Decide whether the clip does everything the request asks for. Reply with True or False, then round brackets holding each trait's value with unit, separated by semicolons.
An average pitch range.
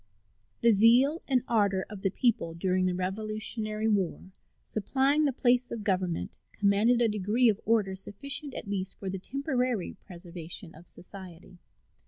True (4.3 semitones)